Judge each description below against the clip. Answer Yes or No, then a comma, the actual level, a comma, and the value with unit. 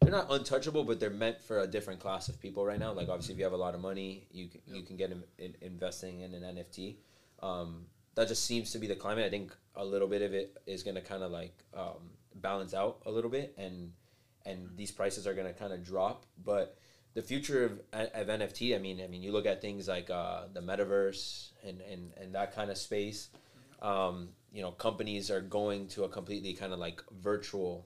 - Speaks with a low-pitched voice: Yes, very low, 95 Hz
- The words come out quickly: Yes, fast, 235 wpm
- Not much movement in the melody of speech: Yes, narrow, 2.3 semitones